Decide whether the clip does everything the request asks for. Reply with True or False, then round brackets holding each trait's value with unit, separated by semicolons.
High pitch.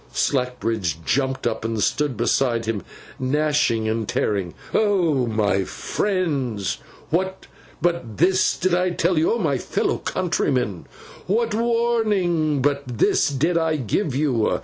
False (145 Hz)